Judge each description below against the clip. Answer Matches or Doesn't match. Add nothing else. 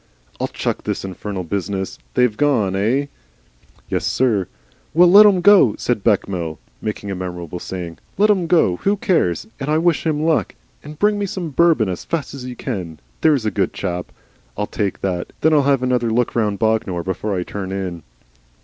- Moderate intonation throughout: Doesn't match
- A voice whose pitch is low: Matches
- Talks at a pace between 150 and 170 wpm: Doesn't match